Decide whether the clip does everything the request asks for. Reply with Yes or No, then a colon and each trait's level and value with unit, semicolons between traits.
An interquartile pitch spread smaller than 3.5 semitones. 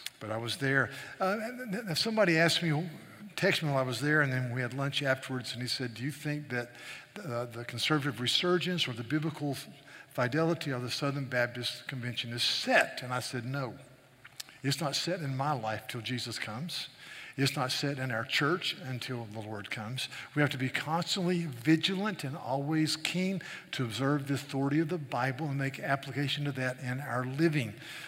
No: average, 3.8 semitones